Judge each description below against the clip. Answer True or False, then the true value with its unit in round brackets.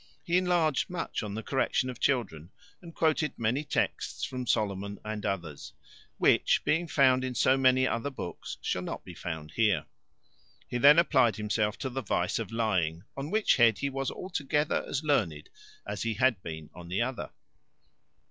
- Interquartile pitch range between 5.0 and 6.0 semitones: True (5.6 semitones)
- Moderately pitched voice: False (120 Hz)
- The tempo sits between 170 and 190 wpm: True (180 wpm)